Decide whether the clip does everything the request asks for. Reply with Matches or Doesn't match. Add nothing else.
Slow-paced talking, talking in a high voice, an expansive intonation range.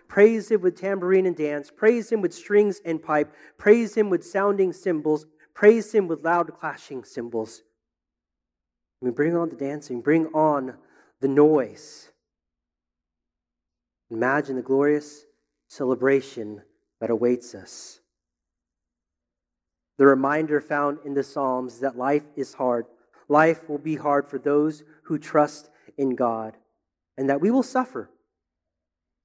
Doesn't match